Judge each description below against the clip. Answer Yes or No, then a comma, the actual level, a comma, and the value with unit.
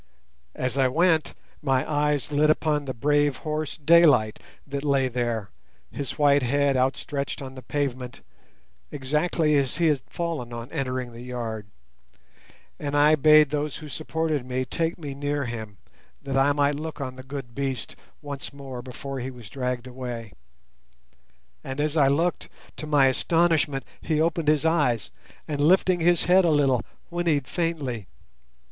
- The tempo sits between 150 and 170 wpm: Yes, average, 155 wpm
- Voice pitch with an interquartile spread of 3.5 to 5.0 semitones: No, average, 3.0 semitones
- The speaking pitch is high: No, medium, 140 Hz